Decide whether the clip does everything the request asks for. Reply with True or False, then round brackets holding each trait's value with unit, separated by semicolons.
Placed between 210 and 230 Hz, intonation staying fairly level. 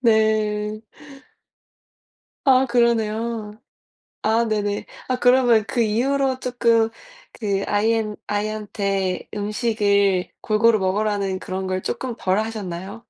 True (215 Hz; 2.3 semitones)